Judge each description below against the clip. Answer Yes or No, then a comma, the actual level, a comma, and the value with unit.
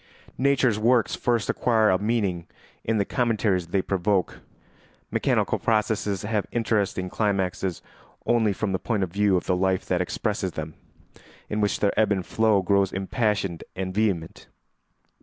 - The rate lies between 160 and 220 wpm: No, average, 150 wpm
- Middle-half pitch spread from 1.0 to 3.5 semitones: Yes, average, 2.8 semitones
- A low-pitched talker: Yes, low, 100 Hz